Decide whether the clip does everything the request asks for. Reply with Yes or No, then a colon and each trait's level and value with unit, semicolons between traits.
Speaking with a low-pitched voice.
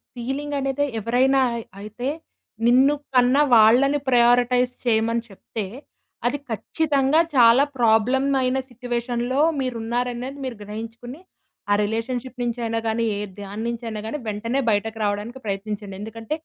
No: high, 240 Hz